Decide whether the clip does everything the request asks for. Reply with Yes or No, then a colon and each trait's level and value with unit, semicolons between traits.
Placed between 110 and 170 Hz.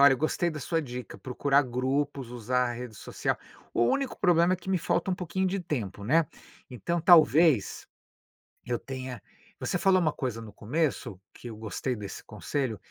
Yes: low, 135 Hz